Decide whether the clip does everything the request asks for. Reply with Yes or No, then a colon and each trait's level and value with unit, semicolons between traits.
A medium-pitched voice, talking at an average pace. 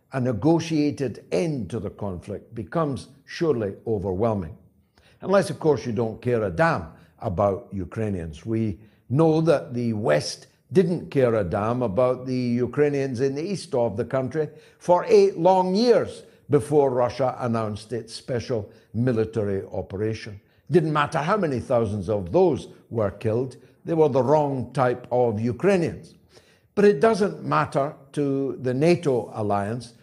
No: low, 125 Hz; average, 145 wpm